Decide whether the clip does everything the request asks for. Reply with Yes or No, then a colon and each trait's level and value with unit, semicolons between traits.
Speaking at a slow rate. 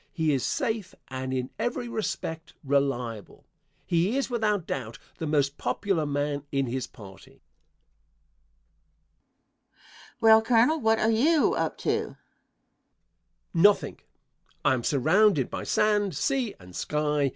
Yes: slow, 130 wpm